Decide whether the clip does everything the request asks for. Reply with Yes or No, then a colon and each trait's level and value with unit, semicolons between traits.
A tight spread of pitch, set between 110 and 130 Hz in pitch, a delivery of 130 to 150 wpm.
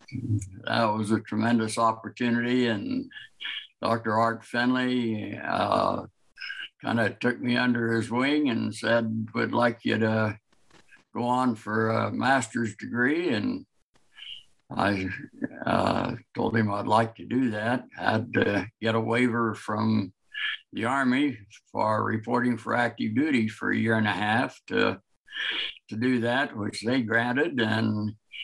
Yes: narrow, 1.9 semitones; low, 115 Hz; average, 145 wpm